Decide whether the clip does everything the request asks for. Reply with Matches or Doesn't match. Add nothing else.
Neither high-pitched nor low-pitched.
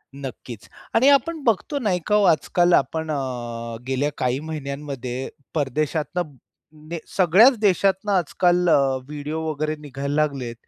Matches